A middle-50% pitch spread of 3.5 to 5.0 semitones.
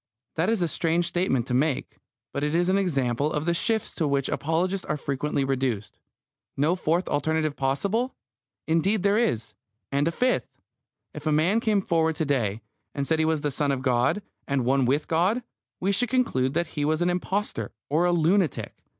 Yes: average, 4.5 semitones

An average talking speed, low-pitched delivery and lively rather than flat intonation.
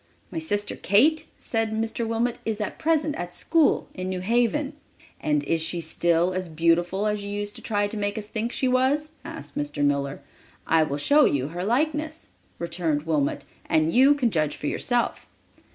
No: average, 185 wpm; high, 205 Hz; wide, 7.4 semitones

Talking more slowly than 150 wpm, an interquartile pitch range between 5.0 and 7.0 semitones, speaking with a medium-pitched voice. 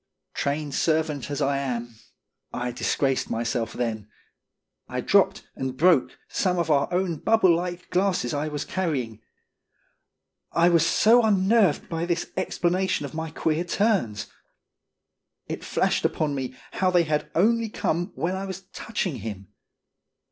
Yes: average, 140 wpm; average, 5.3 semitones; medium, 160 Hz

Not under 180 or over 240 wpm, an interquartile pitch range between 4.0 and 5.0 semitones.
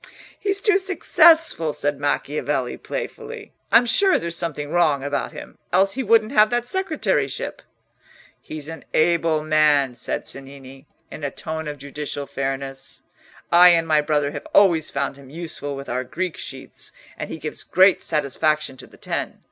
No: average, 160 wpm; average, 4.5 semitones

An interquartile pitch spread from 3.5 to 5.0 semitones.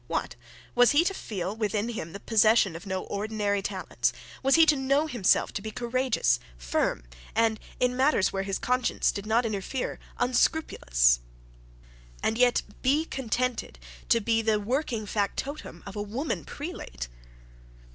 Yes: average, 4.2 semitones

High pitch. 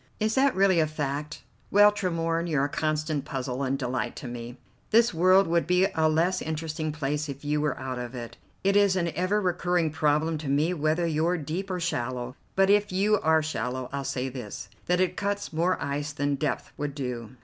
No: medium, 155 Hz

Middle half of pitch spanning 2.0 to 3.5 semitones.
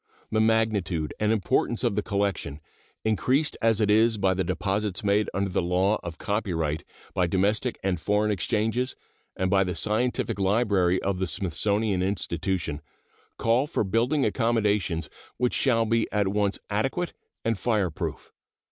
Yes: average, 3.1 semitones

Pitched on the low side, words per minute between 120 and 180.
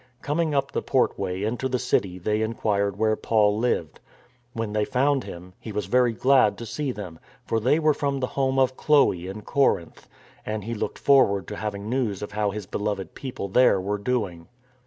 No: low, 110 Hz; average, 195 wpm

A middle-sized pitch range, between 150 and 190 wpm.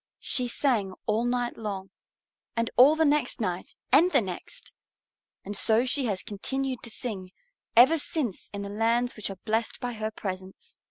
Yes: average, 3.9 semitones; average, 170 wpm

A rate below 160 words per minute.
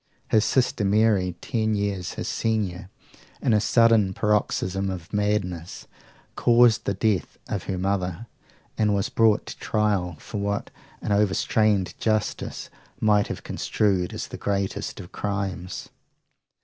Yes: slow, 135 wpm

